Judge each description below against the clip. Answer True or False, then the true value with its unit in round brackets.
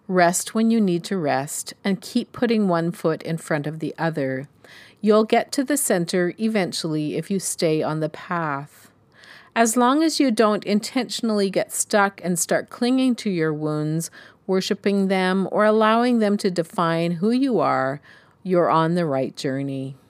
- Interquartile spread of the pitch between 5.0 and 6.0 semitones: True (5.3 semitones)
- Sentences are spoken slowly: False (170 wpm)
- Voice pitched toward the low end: False (185 Hz)